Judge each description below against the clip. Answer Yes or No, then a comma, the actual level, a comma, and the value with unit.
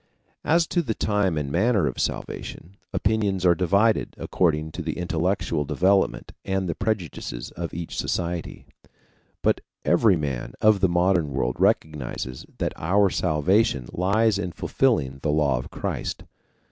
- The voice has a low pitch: Yes, very low, 90 Hz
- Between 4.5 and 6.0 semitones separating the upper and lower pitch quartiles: Yes, average, 4.8 semitones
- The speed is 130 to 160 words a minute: Yes, average, 145 wpm